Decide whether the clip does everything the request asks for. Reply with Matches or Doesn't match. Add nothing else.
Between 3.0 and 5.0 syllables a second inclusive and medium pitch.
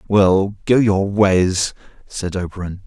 Doesn't match